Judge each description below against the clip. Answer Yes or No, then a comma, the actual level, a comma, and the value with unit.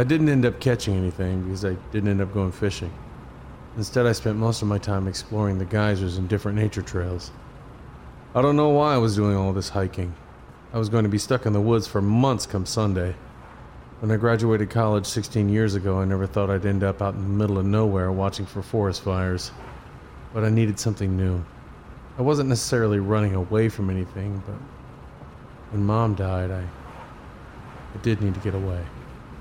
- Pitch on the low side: Yes, low, 100 Hz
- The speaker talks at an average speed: Yes, average, 195 wpm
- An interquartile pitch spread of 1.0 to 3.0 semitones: Yes, narrow, 2.6 semitones